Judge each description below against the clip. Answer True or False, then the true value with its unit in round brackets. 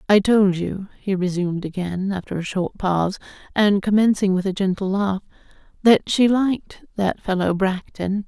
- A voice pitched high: True (195 Hz)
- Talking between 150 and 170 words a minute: True (160 wpm)